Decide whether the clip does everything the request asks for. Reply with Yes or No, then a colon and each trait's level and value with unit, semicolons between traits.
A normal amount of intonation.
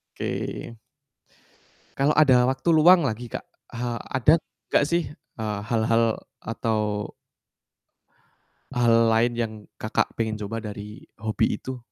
Yes: average, 3.1 semitones